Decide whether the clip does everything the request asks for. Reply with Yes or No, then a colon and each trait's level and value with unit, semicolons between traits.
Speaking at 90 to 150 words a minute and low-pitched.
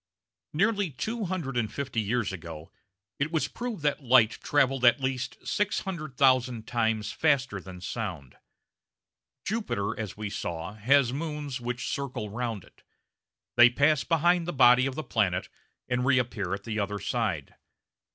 Yes: average, 145 wpm; low, 125 Hz